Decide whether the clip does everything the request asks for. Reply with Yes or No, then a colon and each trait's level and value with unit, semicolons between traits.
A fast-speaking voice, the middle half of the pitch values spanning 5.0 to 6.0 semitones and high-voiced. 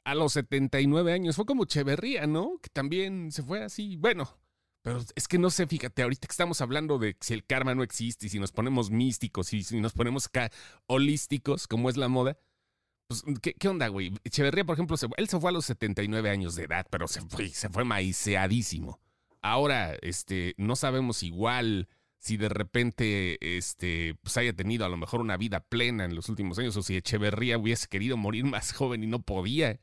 No: fast, 205 wpm; wide, 5.5 semitones; low, 120 Hz